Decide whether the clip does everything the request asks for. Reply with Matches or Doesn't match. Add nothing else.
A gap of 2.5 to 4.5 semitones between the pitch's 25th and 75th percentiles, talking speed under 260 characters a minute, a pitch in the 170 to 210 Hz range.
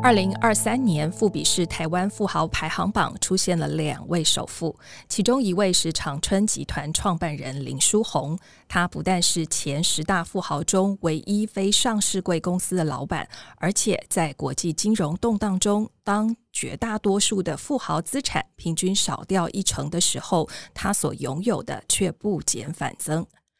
Matches